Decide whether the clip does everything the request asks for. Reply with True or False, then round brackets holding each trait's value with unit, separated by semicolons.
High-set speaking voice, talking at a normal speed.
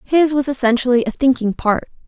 True (260 Hz; 175 wpm)